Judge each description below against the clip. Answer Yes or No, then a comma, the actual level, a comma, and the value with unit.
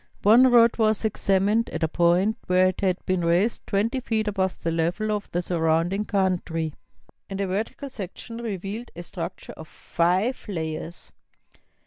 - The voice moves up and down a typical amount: Yes, average, 3.9 semitones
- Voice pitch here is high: Yes, high, 195 Hz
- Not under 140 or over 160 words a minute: Yes, average, 155 wpm